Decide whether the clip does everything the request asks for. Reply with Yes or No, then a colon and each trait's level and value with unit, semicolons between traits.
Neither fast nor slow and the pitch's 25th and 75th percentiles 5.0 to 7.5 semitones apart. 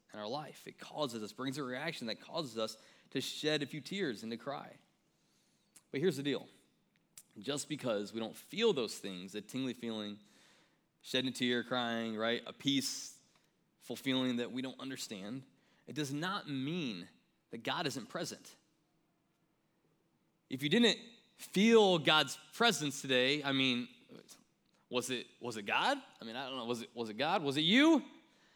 Yes: average, 170 wpm; average, 5.3 semitones